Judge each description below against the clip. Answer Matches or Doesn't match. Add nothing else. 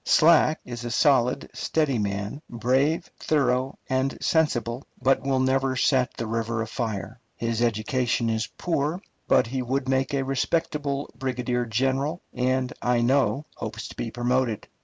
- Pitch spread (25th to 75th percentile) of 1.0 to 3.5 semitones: Matches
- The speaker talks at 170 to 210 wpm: Doesn't match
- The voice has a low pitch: Matches